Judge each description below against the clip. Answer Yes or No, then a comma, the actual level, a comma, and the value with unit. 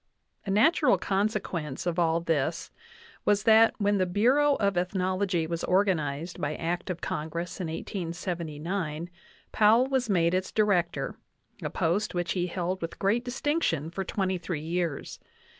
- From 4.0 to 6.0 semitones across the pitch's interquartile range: No, average, 3.5 semitones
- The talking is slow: No, average, 155 wpm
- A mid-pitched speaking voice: Yes, medium, 180 Hz